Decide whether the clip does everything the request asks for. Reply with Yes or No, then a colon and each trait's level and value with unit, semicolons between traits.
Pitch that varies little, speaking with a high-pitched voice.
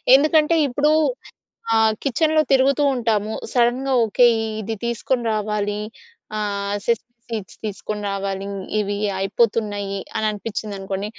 No: average, 3.3 semitones; high, 215 Hz